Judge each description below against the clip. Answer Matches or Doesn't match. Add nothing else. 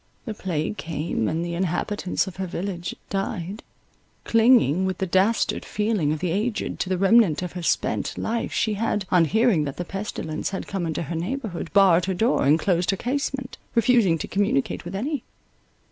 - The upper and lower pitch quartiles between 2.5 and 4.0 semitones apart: Doesn't match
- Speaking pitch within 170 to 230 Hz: Matches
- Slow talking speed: Doesn't match